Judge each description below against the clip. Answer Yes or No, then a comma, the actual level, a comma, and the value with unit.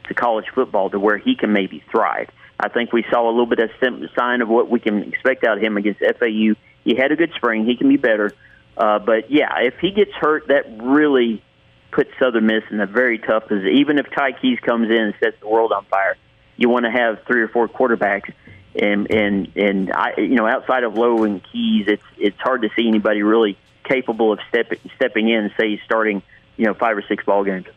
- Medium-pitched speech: No, low, 115 Hz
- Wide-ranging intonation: No, narrow, 2.6 semitones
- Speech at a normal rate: No, fast, 230 wpm